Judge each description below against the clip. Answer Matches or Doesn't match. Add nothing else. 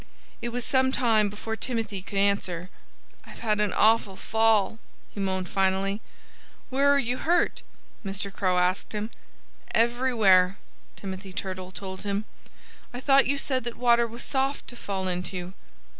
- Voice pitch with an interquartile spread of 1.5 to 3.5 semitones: Doesn't match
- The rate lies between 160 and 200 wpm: Doesn't match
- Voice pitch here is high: Matches